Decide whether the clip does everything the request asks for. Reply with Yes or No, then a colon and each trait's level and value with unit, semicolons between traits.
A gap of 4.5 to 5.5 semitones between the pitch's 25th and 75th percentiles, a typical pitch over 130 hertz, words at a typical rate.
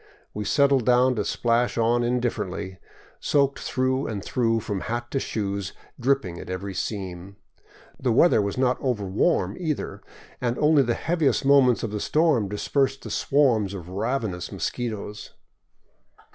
No: average, 4.8 semitones; low, 120 Hz; average, 145 wpm